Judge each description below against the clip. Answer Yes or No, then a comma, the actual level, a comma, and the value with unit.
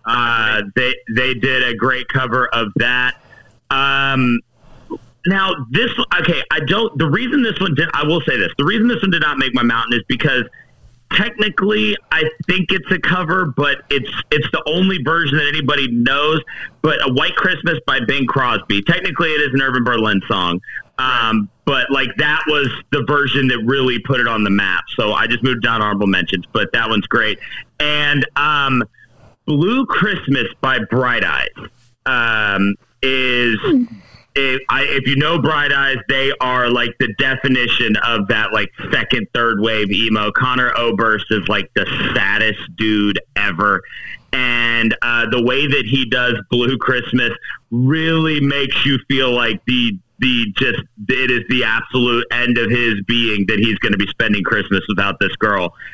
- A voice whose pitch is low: Yes, low, 130 Hz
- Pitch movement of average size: Yes, average, 4.0 semitones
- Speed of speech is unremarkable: Yes, average, 170 wpm